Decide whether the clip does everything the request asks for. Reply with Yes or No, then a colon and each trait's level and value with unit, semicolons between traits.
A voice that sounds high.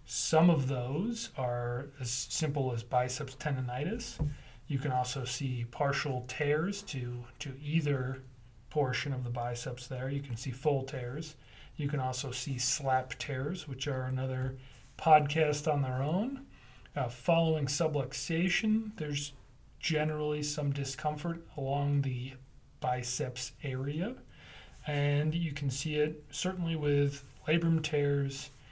No: medium, 140 Hz